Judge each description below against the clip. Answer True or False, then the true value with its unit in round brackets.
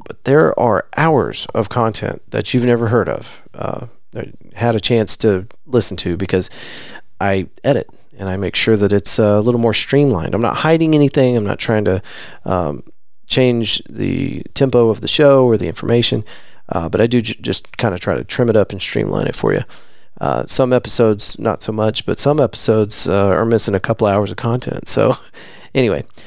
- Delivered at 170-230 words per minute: True (200 wpm)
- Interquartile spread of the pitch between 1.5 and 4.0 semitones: True (3.3 semitones)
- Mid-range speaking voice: False (115 Hz)